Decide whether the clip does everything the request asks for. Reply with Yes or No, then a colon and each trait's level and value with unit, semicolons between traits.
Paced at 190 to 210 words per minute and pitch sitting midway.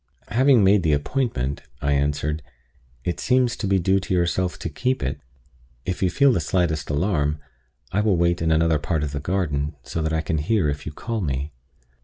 No: average, 200 wpm; very low, 85 Hz